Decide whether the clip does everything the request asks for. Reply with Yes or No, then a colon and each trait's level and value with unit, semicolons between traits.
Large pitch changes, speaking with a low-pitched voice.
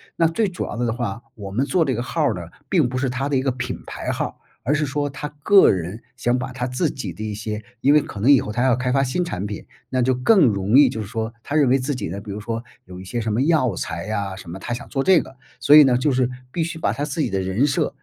No: average, 5.0 semitones; low, 125 Hz